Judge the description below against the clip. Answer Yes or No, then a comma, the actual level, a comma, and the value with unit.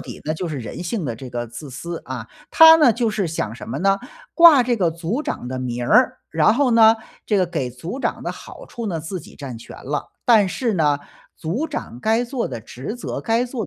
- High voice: No, medium, 180 Hz